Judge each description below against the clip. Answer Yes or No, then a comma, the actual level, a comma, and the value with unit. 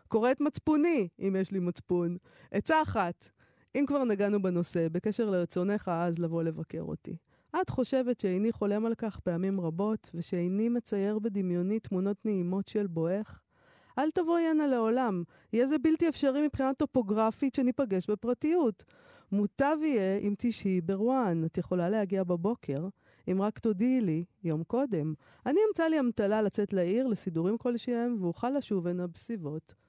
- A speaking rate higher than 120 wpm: Yes, average, 145 wpm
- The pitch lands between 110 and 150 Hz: No, high, 210 Hz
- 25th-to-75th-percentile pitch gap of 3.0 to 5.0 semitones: No, wide, 5.4 semitones